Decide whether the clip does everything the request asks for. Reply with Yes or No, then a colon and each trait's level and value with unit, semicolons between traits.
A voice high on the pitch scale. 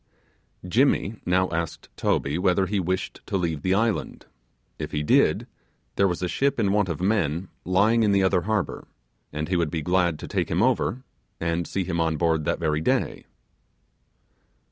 No: very low, 90 Hz